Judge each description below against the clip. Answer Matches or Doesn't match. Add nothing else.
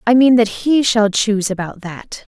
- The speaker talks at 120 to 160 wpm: Doesn't match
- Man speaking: Doesn't match